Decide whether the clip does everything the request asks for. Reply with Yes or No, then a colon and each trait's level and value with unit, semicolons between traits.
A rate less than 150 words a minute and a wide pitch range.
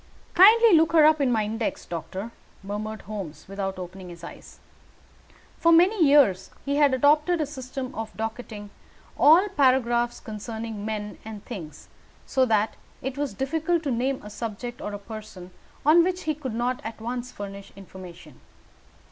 No: average, 160 wpm; wide, 5.9 semitones